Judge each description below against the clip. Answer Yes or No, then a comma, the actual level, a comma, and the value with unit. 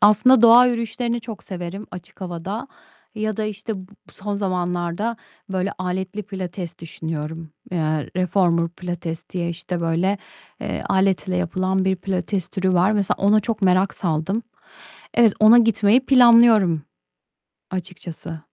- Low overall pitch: No, high, 190 Hz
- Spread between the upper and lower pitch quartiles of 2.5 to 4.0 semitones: Yes, average, 3.3 semitones